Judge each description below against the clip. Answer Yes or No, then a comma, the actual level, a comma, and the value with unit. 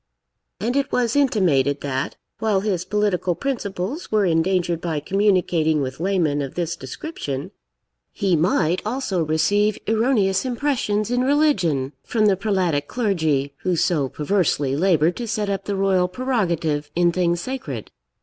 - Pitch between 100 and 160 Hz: No, medium, 185 Hz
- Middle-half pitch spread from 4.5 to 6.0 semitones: Yes, average, 5.1 semitones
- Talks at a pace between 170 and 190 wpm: No, average, 140 wpm